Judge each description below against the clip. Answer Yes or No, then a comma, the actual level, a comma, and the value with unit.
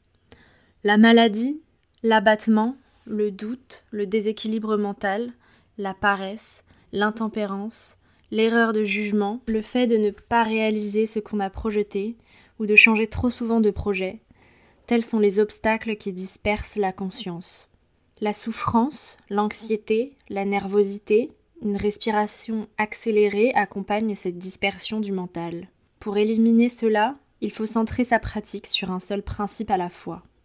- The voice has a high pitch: Yes, high, 215 Hz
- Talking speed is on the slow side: Yes, slow, 130 wpm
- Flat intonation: Yes, narrow, 1.6 semitones